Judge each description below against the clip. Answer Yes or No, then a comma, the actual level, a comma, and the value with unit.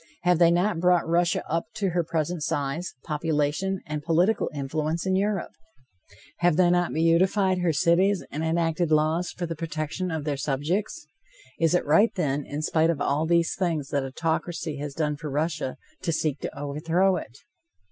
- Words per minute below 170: No, average, 175 wpm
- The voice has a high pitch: No, medium, 165 Hz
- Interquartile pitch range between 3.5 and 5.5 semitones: No, average, 2.8 semitones